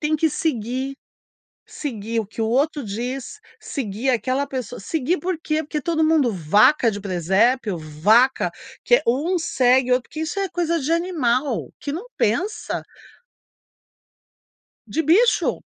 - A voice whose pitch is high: Yes, very high, 265 Hz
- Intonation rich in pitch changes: Yes, wide, 5.8 semitones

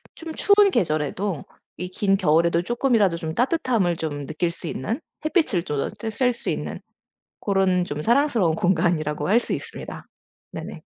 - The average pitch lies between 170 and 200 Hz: Yes, medium, 185 Hz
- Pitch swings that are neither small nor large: No, wide, 6.7 semitones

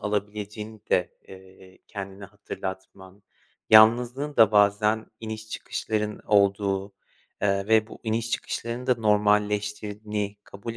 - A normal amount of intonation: No, narrow, 1.6 semitones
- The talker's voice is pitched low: Yes, low, 105 Hz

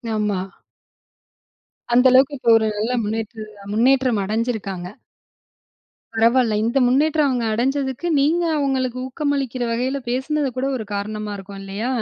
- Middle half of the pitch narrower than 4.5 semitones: Yes, average, 3.7 semitones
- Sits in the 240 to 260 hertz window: Yes, high, 245 Hz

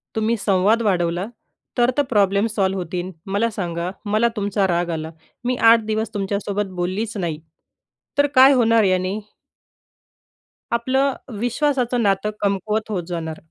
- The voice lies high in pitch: Yes, high, 205 Hz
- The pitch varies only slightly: No, average, 3.7 semitones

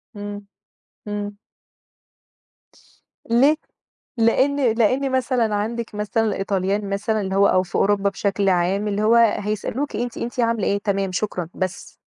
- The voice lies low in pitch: No, high, 210 Hz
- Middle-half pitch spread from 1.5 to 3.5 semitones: Yes, average, 2.7 semitones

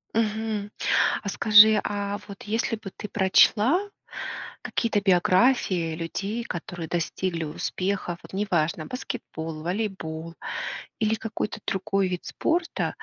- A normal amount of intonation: Yes, average, 3.9 semitones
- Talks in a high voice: Yes, high, 200 Hz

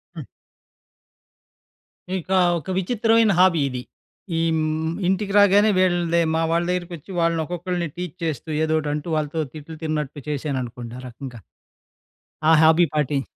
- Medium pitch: Yes, medium, 165 Hz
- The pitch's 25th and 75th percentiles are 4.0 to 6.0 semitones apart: No, average, 3.3 semitones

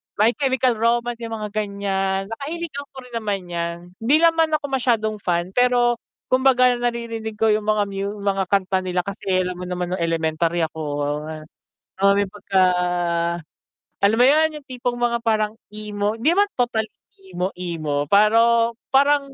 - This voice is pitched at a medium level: No, high, 215 Hz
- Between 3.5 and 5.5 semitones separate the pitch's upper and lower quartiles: Yes, average, 4.1 semitones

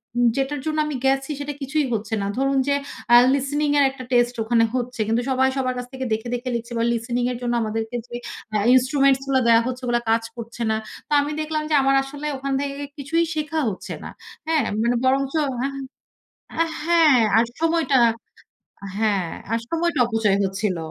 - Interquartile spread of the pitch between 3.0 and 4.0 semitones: Yes, average, 3.5 semitones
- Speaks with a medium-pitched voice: No, very high, 260 Hz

